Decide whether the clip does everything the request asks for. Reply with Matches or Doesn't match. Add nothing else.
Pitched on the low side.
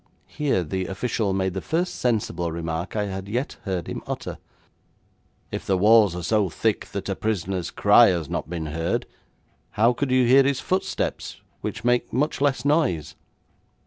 Matches